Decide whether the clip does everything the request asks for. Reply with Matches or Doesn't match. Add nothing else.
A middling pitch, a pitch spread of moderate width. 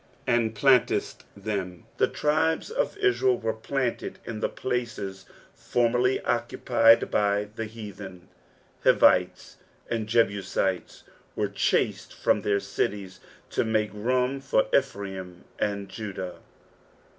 Doesn't match